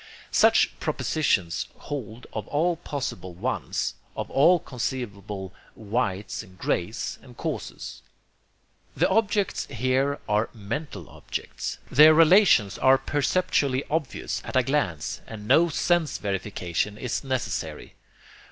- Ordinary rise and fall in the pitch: No, wide, 6.5 semitones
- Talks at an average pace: No, slow, 115 wpm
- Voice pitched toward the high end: No, low, 130 Hz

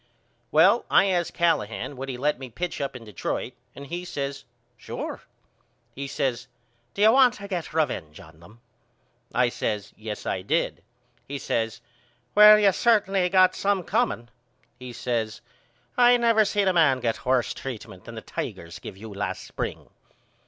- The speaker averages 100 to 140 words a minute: No, average, 165 wpm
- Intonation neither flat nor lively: No, wide, 8.6 semitones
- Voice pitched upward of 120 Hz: Yes, medium, 140 Hz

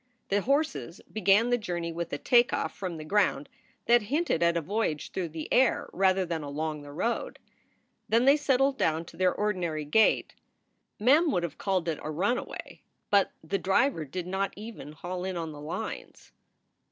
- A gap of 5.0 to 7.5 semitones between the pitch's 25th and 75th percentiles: Yes, wide, 5.4 semitones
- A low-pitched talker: No, medium, 185 Hz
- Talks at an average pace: Yes, average, 180 wpm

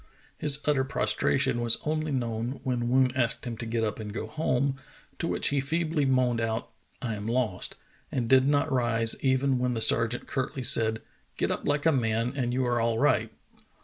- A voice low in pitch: Yes, low, 125 Hz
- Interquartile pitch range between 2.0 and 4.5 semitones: Yes, average, 2.9 semitones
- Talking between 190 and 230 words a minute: Yes, average, 195 wpm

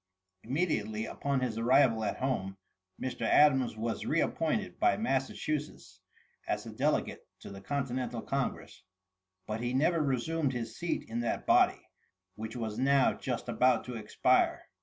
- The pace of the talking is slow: No, average, 145 wpm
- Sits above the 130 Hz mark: No, low, 125 Hz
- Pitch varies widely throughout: No, average, 3.7 semitones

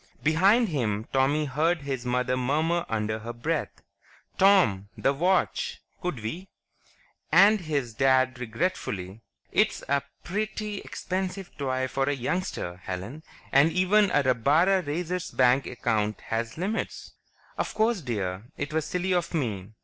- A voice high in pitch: No, medium, 140 Hz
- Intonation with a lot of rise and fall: Yes, wide, 7.2 semitones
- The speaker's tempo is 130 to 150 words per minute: Yes, slow, 135 wpm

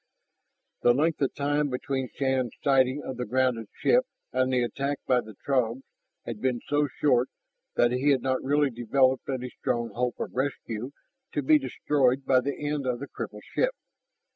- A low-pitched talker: Yes, low, 130 Hz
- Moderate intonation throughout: No, narrow, 2.3 semitones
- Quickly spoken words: No, average, 175 wpm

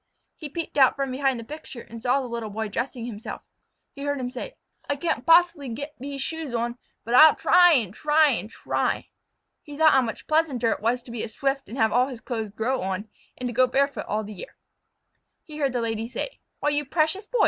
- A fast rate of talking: Yes, fast, 225 wpm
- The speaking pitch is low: No, very high, 260 Hz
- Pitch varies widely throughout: No, average, 4.2 semitones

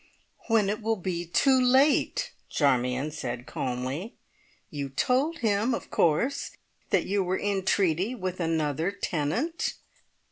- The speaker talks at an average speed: No, slow, 130 wpm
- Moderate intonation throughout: No, wide, 7.5 semitones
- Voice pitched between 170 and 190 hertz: Yes, medium, 185 Hz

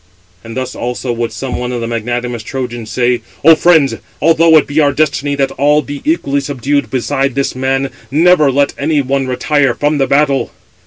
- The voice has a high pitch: No, low, 135 Hz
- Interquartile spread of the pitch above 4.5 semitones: No, average, 2.9 semitones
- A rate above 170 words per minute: Yes, average, 190 wpm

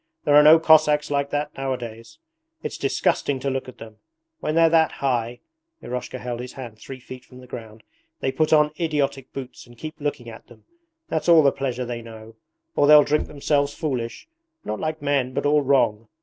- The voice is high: No, low, 135 Hz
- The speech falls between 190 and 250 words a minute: Yes, average, 195 wpm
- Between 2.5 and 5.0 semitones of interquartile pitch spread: Yes, average, 3.6 semitones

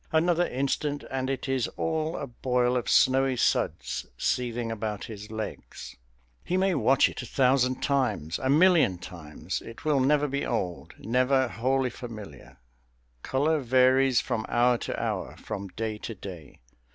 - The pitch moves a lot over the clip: No, average, 3.8 semitones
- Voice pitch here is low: Yes, low, 125 Hz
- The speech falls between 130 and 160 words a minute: Yes, average, 150 wpm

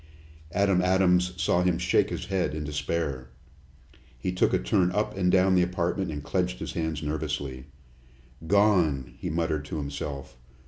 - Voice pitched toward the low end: Yes, very low, 85 Hz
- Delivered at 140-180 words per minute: Yes, average, 155 wpm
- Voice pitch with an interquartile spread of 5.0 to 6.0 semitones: No, average, 3.8 semitones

